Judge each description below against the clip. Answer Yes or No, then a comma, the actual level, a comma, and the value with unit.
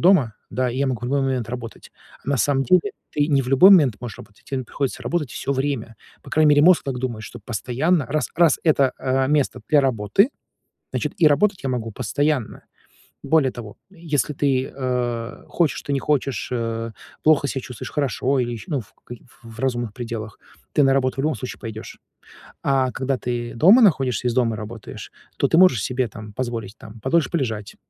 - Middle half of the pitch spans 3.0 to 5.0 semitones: Yes, average, 3.6 semitones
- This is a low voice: Yes, low, 130 Hz